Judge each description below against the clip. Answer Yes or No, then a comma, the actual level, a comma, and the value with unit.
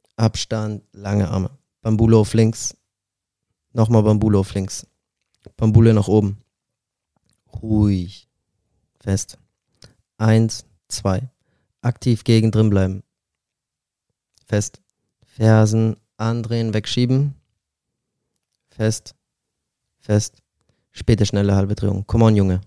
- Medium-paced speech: No, slow, 90 wpm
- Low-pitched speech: Yes, low, 110 Hz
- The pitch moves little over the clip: Yes, narrow, 2.2 semitones